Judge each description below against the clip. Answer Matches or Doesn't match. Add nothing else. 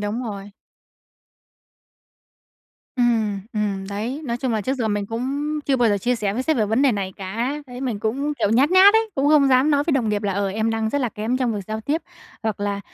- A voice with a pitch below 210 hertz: Doesn't match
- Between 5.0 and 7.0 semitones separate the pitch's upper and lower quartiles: Doesn't match